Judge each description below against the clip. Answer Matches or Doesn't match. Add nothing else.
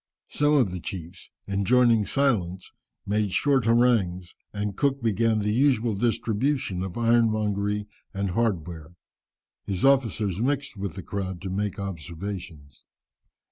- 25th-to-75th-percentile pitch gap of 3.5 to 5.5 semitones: Matches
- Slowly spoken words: Matches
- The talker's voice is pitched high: Doesn't match